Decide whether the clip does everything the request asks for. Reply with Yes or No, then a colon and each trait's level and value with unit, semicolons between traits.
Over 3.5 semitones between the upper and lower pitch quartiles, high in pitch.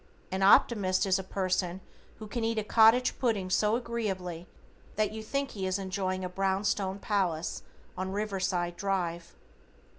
No: narrow, 2.5 semitones; high, 195 Hz